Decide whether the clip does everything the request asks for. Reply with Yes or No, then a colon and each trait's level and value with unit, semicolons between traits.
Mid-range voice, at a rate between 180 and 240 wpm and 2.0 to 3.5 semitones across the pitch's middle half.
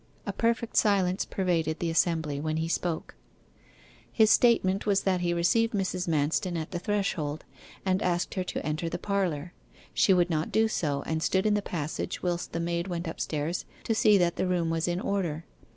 Yes: medium, 175 Hz; average, 190 wpm; average, 3.0 semitones